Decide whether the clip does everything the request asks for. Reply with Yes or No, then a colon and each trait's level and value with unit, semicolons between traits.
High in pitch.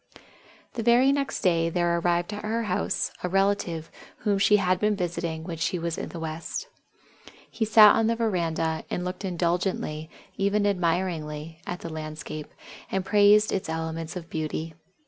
No: medium, 175 Hz